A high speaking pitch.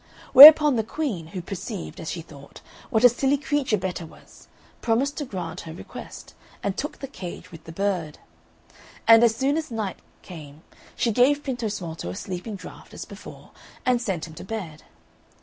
Yes: high, 210 Hz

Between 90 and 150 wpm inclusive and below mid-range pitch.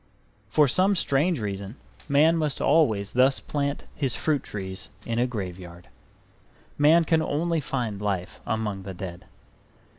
Yes: average, 140 wpm; low, 125 Hz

